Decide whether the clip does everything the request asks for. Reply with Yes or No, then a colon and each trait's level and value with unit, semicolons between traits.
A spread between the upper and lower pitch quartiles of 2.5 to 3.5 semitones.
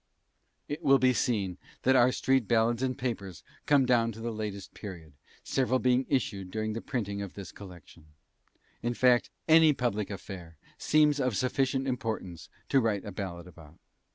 No: average, 4.7 semitones